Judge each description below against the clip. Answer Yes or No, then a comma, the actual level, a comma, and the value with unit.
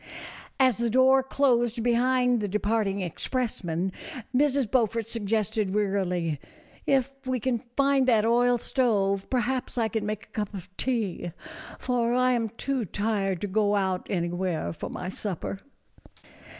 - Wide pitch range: No, average, 4.2 semitones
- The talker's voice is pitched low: No, high, 225 Hz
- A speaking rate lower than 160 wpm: Yes, average, 150 wpm